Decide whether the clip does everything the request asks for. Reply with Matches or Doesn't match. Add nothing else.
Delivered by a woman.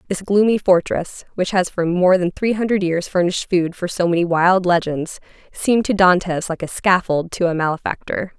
Matches